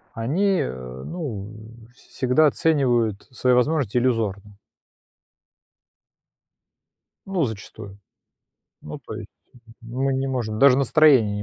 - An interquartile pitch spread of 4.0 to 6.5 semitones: Yes, average, 5.0 semitones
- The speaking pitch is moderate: No, low, 125 Hz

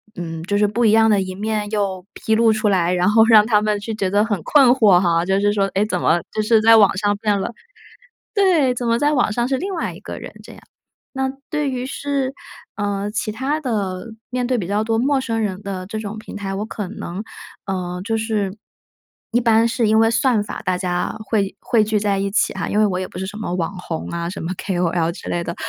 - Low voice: No, high, 210 Hz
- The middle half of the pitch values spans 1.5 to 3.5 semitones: Yes, average, 3.1 semitones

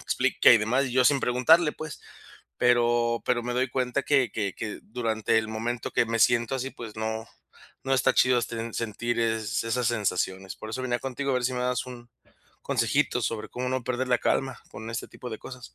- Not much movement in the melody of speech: Yes, narrow, 2.1 semitones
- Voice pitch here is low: Yes, low, 120 Hz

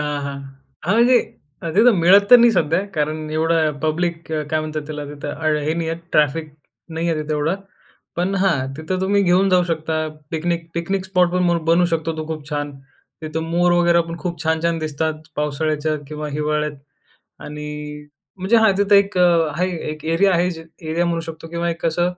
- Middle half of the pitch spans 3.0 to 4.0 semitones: No, narrow, 2.4 semitones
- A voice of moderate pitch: Yes, medium, 165 Hz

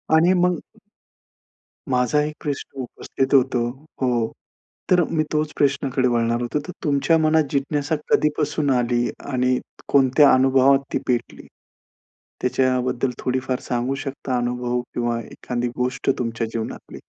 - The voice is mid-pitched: No, low, 130 Hz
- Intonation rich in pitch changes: No, narrow, 2.6 semitones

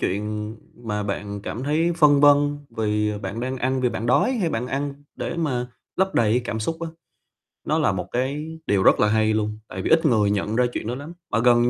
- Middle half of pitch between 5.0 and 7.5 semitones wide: Yes, average, 5.3 semitones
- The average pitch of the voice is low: Yes, low, 120 Hz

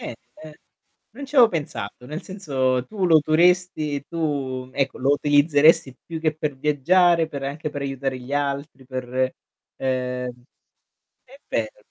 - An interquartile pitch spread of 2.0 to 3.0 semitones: No, average, 3.7 semitones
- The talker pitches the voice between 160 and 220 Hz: No, medium, 145 Hz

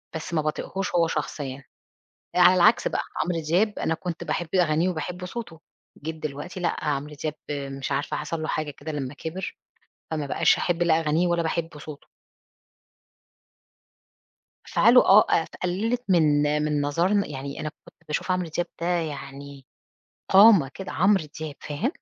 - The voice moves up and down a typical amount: Yes, average, 3.3 semitones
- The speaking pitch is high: No, medium, 160 Hz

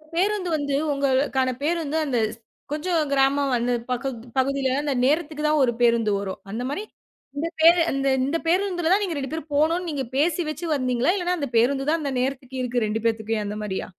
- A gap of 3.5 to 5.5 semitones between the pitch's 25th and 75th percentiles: Yes, average, 4.1 semitones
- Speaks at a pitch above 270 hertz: Yes, very high, 280 Hz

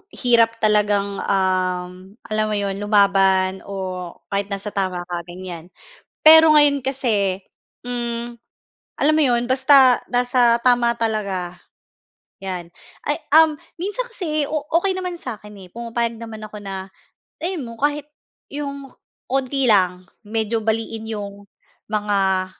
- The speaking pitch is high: Yes, high, 220 Hz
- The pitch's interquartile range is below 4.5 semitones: No, average, 5.0 semitones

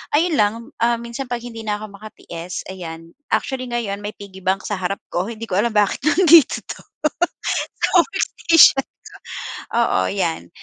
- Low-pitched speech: No, high, 215 Hz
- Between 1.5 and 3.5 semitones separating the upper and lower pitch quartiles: No, average, 4.2 semitones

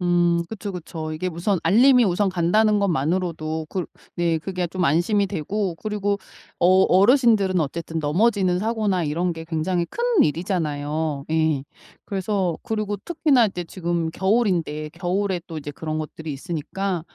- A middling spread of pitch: Yes, average, 3.8 semitones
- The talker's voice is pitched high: No, medium, 180 Hz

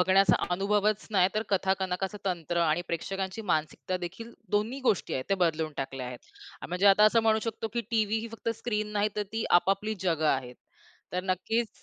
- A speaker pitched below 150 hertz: No, high, 195 Hz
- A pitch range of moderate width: Yes, average, 3.5 semitones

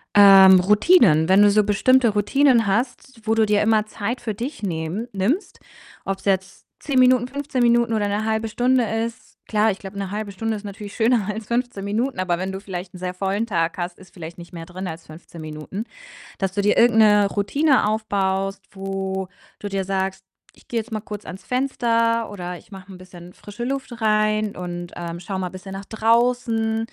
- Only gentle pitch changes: No, average, 3.2 semitones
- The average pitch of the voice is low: No, high, 205 Hz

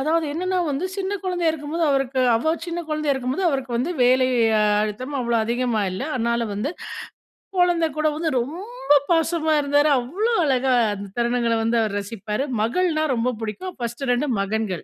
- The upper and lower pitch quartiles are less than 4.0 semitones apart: No, wide, 5.6 semitones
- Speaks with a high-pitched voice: Yes, very high, 270 Hz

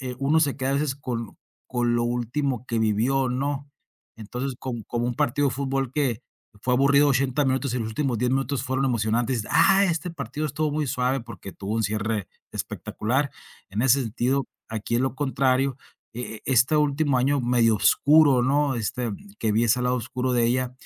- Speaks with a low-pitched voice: Yes, low, 130 Hz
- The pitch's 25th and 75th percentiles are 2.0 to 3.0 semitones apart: Yes, average, 2.7 semitones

